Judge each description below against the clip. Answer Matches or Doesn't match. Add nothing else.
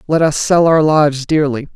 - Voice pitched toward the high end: Doesn't match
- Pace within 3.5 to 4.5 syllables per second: Doesn't match